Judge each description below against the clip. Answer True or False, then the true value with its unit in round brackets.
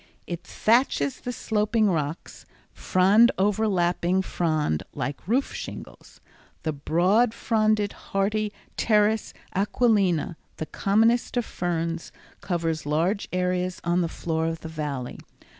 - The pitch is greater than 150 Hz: True (185 Hz)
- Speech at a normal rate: False (115 wpm)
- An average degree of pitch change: True (4.6 semitones)